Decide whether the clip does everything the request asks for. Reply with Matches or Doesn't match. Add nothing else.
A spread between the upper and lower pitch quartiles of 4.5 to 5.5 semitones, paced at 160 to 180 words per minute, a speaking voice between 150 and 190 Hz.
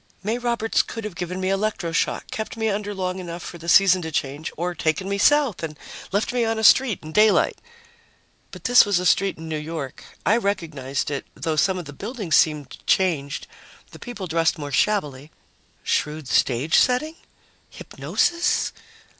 Matches